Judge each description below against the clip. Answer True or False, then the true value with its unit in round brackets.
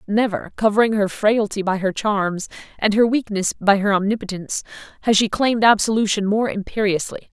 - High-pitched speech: True (205 Hz)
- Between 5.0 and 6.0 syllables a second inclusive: True (5.4 syllables/s)